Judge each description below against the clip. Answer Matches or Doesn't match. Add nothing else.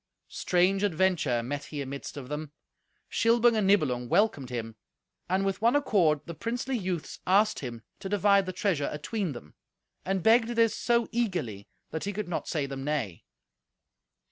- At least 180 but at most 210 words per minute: Doesn't match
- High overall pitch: Doesn't match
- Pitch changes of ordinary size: Doesn't match